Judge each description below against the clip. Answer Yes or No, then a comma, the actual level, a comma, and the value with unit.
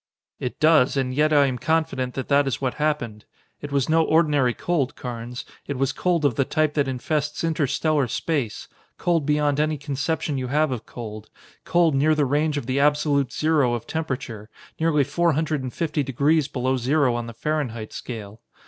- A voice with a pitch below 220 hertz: Yes, medium, 140 Hz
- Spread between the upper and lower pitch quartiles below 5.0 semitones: Yes, average, 3.3 semitones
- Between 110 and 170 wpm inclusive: No, average, 185 wpm